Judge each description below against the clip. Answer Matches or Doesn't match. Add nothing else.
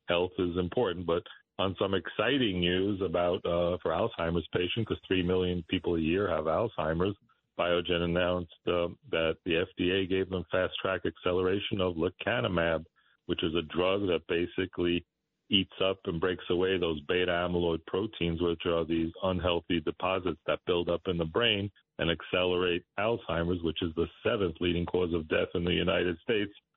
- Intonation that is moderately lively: Doesn't match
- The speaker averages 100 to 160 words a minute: Doesn't match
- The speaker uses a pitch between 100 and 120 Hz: Doesn't match